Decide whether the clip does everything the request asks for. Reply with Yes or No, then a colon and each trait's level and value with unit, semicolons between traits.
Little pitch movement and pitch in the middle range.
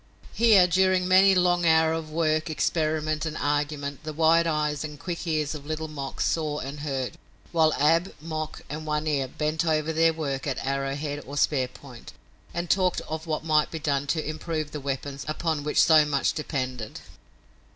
Yes: narrow, 2.0 semitones; medium, 155 Hz